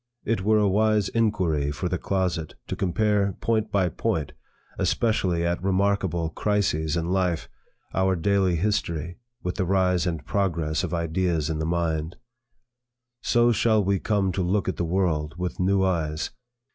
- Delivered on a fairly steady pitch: No, average, 3.2 semitones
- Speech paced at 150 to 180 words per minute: Yes, average, 160 wpm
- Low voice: Yes, very low, 90 Hz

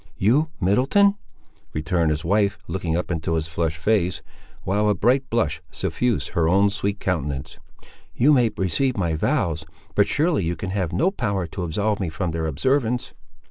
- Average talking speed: Yes, average, 170 wpm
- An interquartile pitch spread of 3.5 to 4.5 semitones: No, average, 5.2 semitones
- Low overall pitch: Yes, very low, 95 Hz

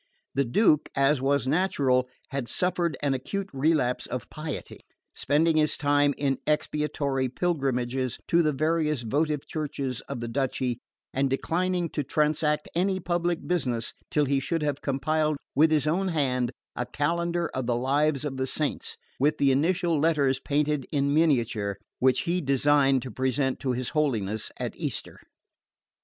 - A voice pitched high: No, medium, 145 Hz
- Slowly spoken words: No, average, 155 wpm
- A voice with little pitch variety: No, average, 3.0 semitones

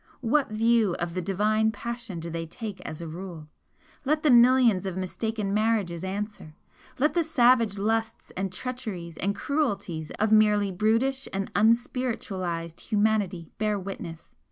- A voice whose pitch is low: No, high, 210 Hz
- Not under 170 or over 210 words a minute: No, average, 145 wpm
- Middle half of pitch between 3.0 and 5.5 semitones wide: Yes, average, 4.2 semitones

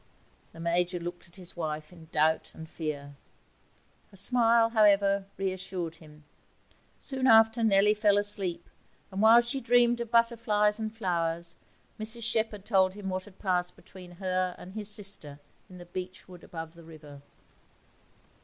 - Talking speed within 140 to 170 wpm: Yes, average, 150 wpm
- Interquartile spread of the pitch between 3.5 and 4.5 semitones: Yes, average, 4.0 semitones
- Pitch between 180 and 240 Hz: Yes, high, 190 Hz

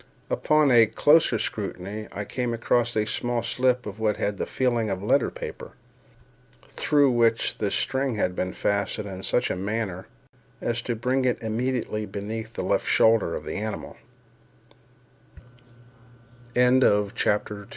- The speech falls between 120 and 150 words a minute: Yes, average, 140 wpm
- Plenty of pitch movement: No, average, 3.1 semitones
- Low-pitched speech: Yes, low, 115 Hz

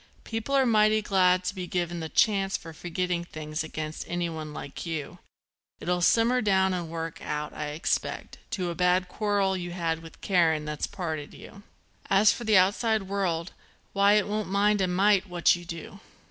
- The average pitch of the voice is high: No, medium, 180 Hz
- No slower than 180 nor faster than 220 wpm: Yes, average, 185 wpm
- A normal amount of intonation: Yes, average, 3.5 semitones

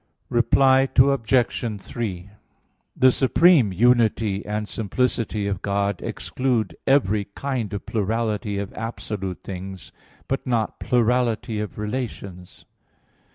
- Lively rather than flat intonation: No, average, 3.7 semitones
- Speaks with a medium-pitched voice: No, low, 110 Hz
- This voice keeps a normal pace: No, slow, 105 wpm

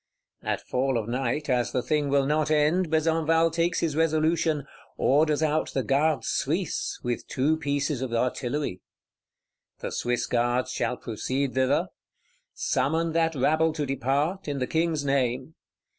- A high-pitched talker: No, medium, 145 Hz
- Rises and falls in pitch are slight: No, average, 3.6 semitones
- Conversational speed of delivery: Yes, average, 145 wpm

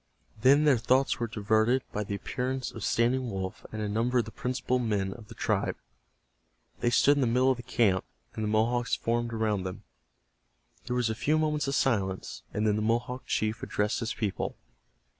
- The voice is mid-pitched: No, low, 115 Hz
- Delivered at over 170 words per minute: Yes, average, 195 wpm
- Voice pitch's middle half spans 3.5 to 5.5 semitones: No, average, 3.0 semitones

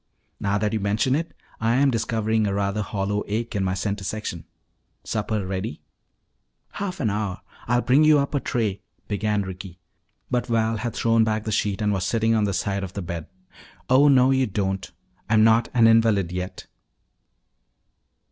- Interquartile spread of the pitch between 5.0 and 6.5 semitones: No, average, 2.7 semitones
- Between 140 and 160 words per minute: No, average, 180 wpm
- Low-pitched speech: Yes, low, 110 Hz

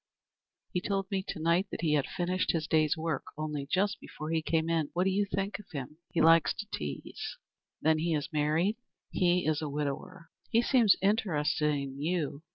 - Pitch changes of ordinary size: Yes, average, 3.6 semitones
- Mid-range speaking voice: Yes, medium, 165 Hz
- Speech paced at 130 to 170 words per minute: No, average, 195 wpm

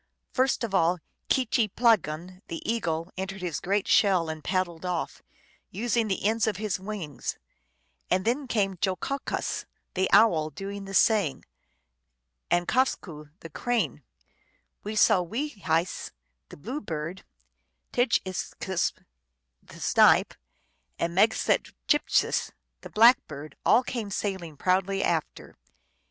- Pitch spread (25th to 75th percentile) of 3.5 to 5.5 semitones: Yes, average, 4.4 semitones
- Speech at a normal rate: No, slow, 130 wpm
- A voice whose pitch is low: No, high, 195 Hz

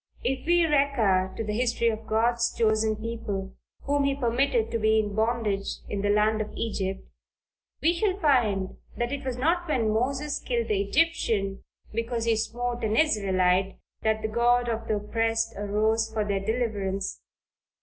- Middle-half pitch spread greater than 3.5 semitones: No, average, 2.8 semitones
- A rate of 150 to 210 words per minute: Yes, average, 165 wpm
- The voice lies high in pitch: Yes, high, 225 Hz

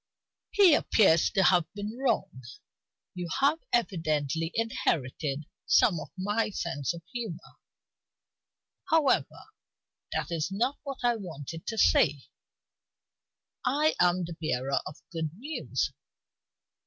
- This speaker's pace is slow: Yes, slow, 115 wpm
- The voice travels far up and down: Yes, wide, 6.7 semitones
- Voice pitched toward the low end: No, medium, 180 Hz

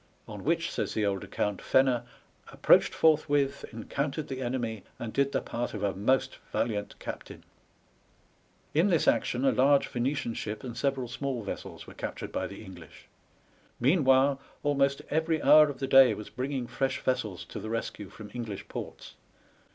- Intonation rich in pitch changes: No, average, 3.9 semitones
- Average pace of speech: Yes, average, 170 wpm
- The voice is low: Yes, low, 130 Hz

